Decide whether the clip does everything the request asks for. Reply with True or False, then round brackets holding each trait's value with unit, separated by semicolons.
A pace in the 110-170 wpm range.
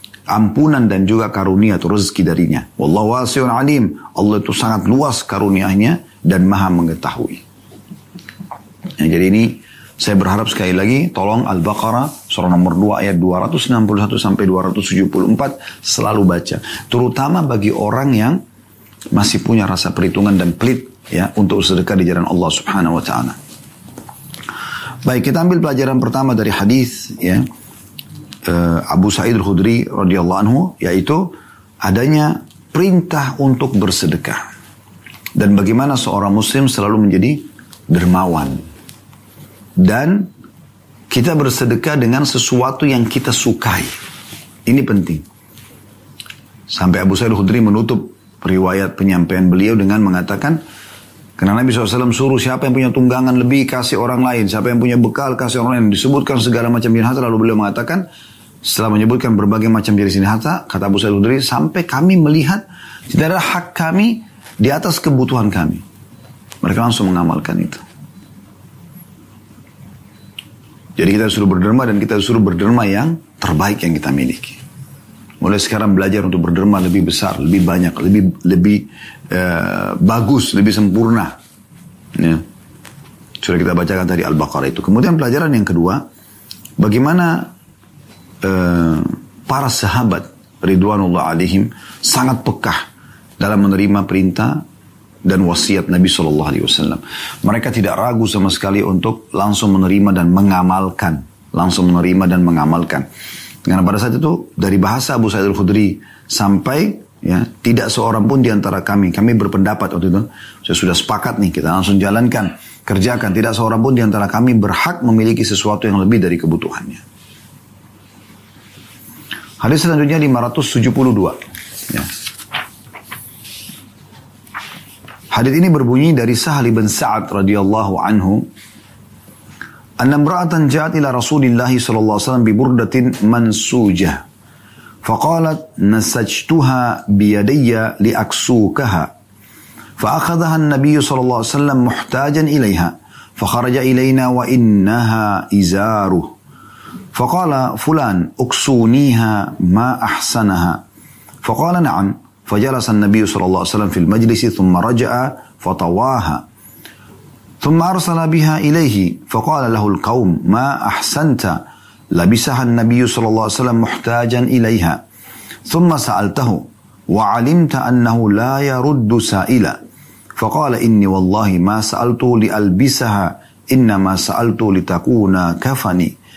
True (120 wpm)